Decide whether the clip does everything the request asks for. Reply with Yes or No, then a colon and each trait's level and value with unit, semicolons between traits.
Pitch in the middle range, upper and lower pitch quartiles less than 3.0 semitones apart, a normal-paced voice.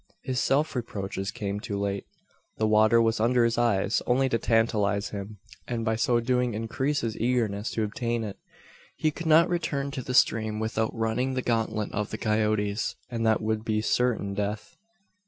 No: low, 110 Hz; narrow, 2.6 semitones; average, 180 wpm